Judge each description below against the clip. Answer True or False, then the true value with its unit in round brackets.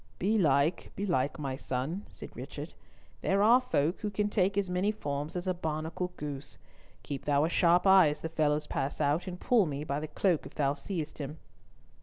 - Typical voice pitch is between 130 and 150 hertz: False (160 Hz)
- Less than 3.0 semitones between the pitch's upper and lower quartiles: False (4.5 semitones)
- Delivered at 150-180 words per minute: False (195 wpm)